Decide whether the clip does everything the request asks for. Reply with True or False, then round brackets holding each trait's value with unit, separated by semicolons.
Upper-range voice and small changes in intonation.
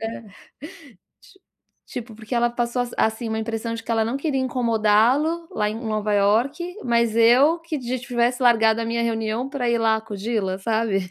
True (230 Hz; 2.0 semitones)